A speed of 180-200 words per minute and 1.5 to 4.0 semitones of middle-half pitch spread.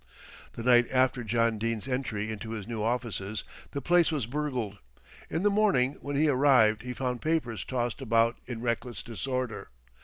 No: average, 165 wpm; average, 2.9 semitones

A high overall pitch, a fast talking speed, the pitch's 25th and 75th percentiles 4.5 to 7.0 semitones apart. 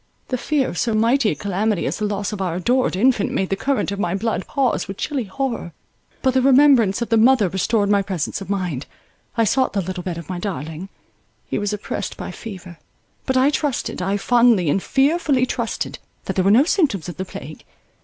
Yes: high, 210 Hz; fast, 215 wpm; average, 5.2 semitones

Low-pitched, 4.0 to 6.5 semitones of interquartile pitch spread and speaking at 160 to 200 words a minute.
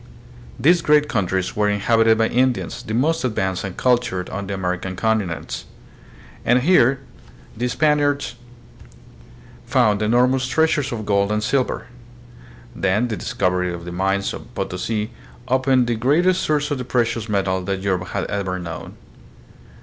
No: low, 110 Hz; average, 5.0 semitones; average, 150 wpm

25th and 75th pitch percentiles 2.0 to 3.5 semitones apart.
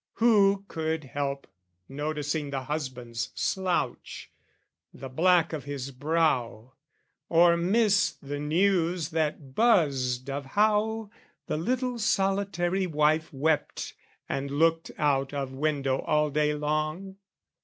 No: average, 4.8 semitones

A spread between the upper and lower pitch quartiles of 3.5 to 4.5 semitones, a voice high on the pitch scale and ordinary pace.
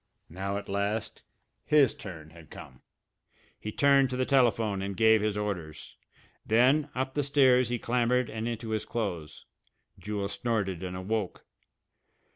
No: average, 4.2 semitones; low, 110 Hz; average, 145 wpm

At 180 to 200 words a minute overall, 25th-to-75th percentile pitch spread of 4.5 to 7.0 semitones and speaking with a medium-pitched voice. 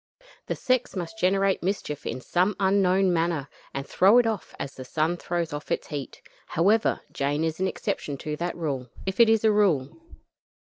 Yes: average, 185 wpm; average, 4.9 semitones; medium, 175 Hz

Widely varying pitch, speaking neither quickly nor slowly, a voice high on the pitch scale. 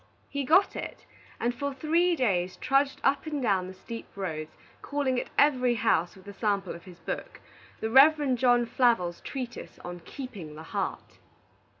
Yes: wide, 6.8 semitones; average, 170 wpm; high, 240 Hz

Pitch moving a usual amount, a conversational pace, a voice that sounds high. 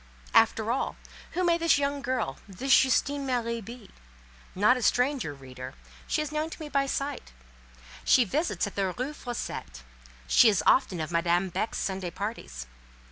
No: wide, 7.2 semitones; average, 165 wpm; high, 235 Hz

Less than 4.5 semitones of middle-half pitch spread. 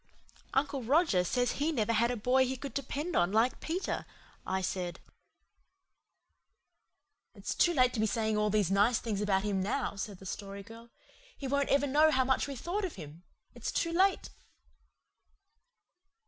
No: wide, 5.6 semitones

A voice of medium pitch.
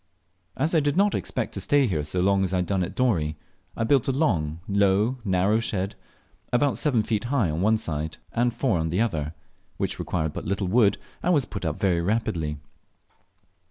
No: low, 100 Hz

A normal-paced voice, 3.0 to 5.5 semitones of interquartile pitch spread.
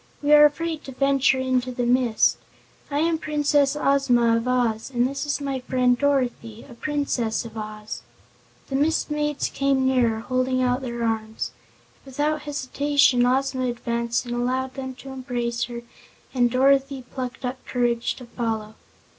No: average, 155 wpm; narrow, 2.5 semitones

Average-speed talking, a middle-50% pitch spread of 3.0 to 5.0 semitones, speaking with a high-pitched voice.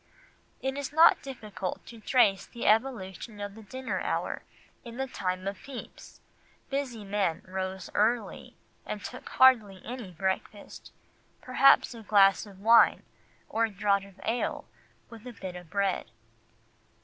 Yes: average, 145 wpm; average, 4.0 semitones; high, 210 Hz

